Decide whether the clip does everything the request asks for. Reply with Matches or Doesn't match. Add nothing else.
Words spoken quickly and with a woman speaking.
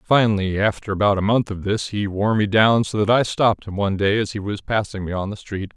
Doesn't match